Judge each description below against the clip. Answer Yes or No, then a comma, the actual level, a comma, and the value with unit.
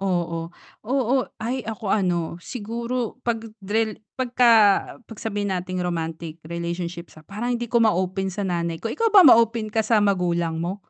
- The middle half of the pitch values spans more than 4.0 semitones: Yes, average, 5.1 semitones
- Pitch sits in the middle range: No, high, 200 Hz